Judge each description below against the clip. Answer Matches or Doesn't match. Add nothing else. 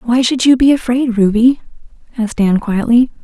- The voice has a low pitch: Doesn't match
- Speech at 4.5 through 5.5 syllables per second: Doesn't match